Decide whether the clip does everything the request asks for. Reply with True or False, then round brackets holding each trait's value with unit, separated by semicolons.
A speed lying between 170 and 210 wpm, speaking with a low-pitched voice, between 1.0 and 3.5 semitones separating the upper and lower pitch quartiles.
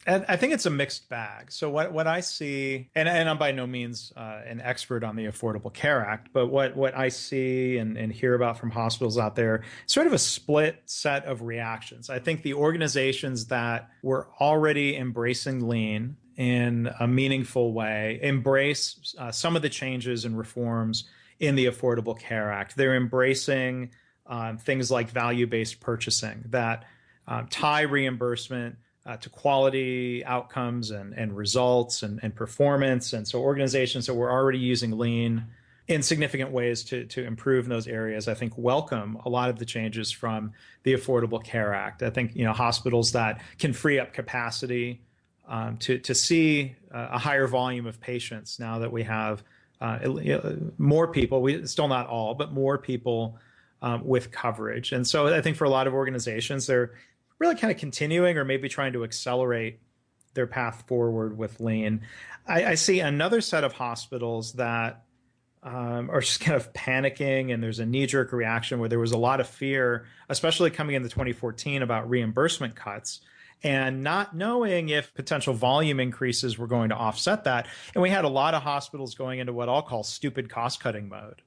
True (180 wpm; 125 Hz; 2.8 semitones)